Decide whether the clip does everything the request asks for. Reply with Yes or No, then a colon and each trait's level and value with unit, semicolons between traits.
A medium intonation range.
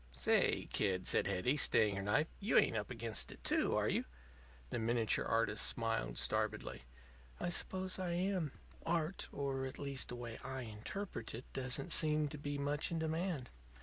No: wide, 6.1 semitones